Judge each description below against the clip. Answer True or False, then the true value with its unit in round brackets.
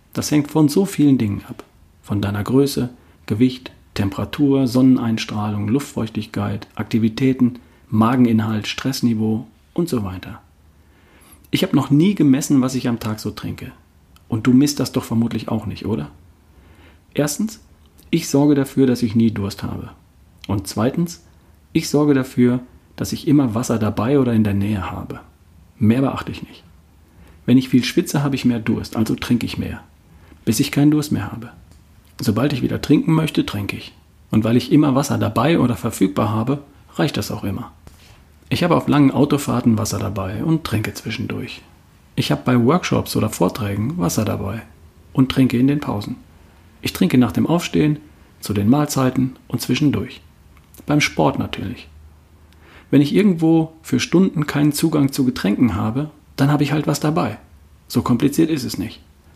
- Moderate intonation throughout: False (6.6 semitones)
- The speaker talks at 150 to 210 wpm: True (165 wpm)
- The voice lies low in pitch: True (115 Hz)